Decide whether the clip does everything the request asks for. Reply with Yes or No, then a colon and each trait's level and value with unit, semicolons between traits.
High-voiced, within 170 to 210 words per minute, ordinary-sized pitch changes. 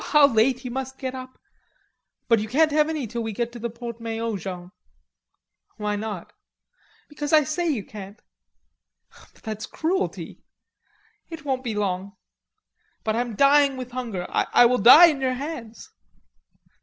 No: high, 245 Hz; average, 160 wpm; average, 4.4 semitones